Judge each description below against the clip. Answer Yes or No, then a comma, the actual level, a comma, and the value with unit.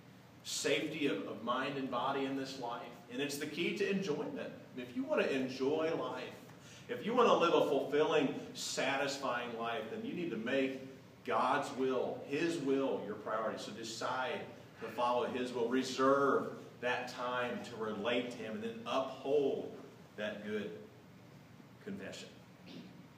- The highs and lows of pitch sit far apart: No, average, 2.9 semitones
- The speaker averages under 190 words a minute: Yes, average, 155 wpm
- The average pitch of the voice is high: No, low, 135 Hz